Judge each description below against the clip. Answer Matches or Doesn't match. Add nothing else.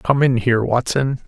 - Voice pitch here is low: Matches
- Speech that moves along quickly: Doesn't match